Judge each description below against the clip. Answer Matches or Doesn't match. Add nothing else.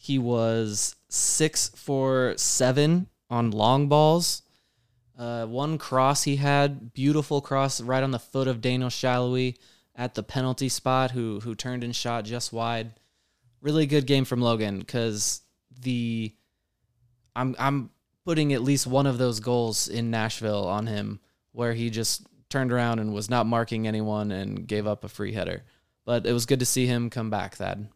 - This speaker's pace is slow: Doesn't match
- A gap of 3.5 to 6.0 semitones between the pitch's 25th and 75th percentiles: Doesn't match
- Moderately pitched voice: Doesn't match